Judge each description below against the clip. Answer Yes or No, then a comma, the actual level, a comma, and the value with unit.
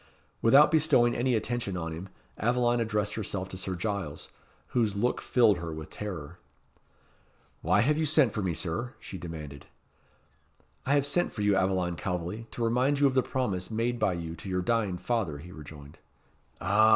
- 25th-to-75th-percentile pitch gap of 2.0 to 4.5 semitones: No, average, 5.3 semitones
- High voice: No, low, 105 Hz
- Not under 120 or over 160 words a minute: No, average, 175 wpm